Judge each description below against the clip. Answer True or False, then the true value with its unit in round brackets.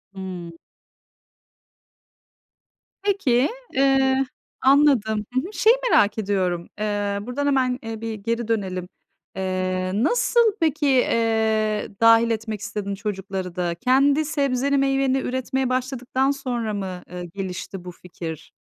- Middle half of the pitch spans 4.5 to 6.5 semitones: True (5.6 semitones)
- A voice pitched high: True (225 Hz)